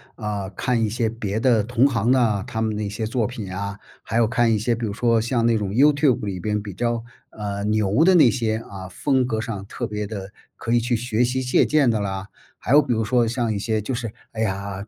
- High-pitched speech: No, low, 110 Hz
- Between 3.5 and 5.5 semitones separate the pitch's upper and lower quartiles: No, average, 2.7 semitones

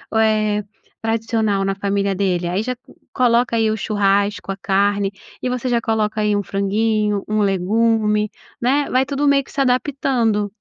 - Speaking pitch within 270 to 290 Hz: No, high, 215 Hz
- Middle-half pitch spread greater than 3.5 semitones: No, average, 2.7 semitones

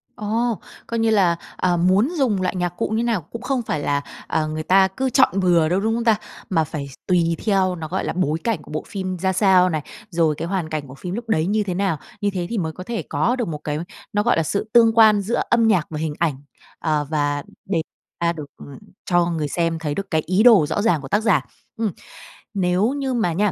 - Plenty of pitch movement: No, average, 5.0 semitones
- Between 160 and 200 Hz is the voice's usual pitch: Yes, medium, 185 Hz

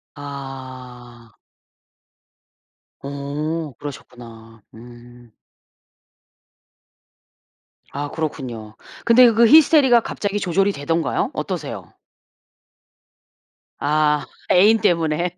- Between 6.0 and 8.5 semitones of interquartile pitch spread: Yes, wide, 6.4 semitones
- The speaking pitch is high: No, medium, 145 Hz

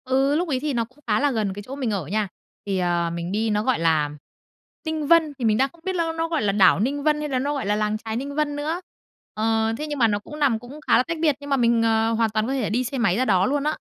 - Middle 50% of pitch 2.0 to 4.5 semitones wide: No, wide, 5.4 semitones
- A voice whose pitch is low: No, high, 245 Hz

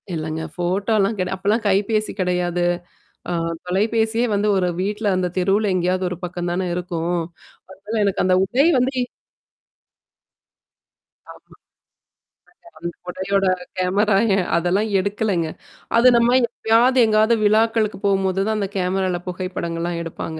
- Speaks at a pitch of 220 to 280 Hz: No, high, 190 Hz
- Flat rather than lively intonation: No, average, 3.2 semitones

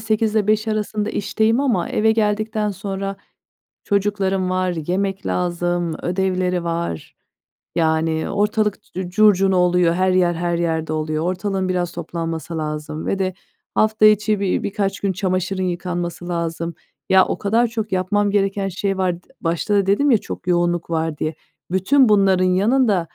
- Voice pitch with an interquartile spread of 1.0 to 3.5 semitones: Yes, average, 3.1 semitones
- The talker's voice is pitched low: No, medium, 185 Hz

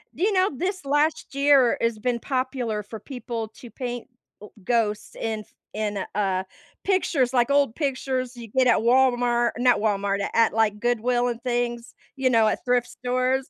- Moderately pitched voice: No, high, 245 Hz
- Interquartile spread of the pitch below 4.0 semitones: Yes, average, 2.8 semitones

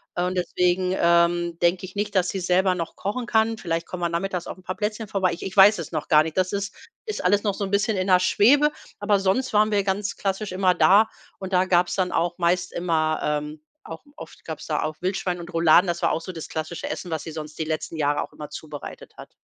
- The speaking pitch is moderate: Yes, medium, 180 Hz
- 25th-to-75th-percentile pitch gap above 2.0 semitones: Yes, average, 2.8 semitones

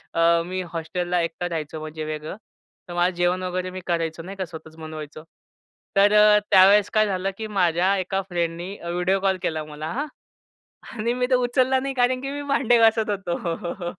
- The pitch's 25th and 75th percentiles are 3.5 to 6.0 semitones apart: Yes, average, 3.9 semitones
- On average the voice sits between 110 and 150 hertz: No, medium, 185 Hz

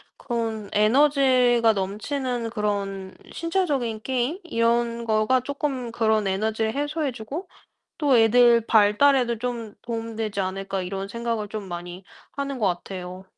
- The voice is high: Yes, high, 230 Hz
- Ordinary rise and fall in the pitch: Yes, average, 3.5 semitones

